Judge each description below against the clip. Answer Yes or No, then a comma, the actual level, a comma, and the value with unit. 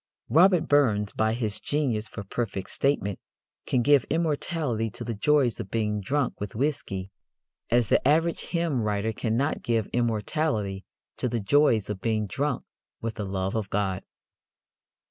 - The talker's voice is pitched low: Yes, low, 115 Hz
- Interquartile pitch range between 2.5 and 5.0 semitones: No, wide, 5.6 semitones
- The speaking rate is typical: Yes, average, 150 wpm